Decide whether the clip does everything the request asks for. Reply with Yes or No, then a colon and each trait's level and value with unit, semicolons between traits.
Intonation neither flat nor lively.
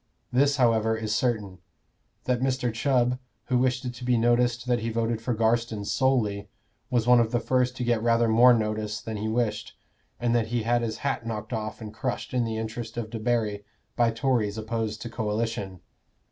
No: narrow, 2.0 semitones